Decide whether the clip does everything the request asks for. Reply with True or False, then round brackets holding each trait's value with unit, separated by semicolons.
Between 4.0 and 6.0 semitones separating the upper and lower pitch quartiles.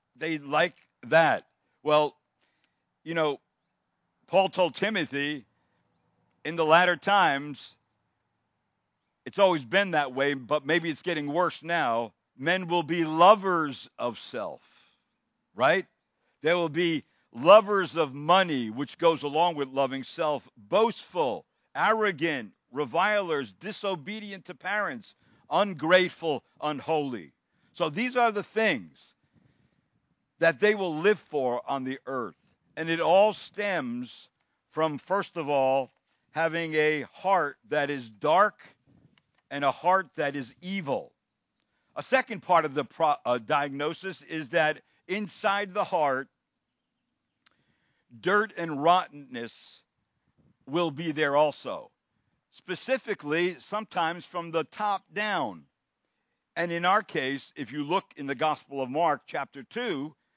True (5.0 semitones)